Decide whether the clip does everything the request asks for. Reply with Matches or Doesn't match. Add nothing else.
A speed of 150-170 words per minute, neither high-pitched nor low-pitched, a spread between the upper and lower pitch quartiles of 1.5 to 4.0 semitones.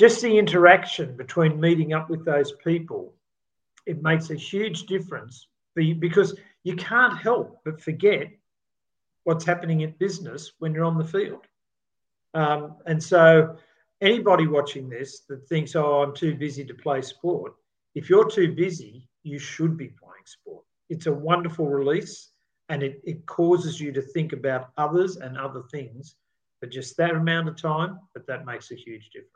Matches